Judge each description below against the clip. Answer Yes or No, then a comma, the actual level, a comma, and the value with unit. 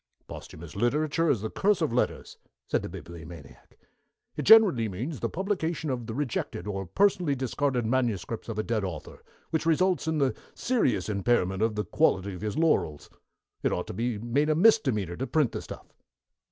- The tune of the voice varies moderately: No, wide, 7.5 semitones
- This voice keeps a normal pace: Yes, average, 180 wpm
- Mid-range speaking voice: No, low, 120 Hz